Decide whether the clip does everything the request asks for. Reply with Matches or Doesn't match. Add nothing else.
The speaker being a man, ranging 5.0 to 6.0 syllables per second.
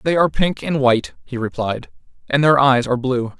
Matches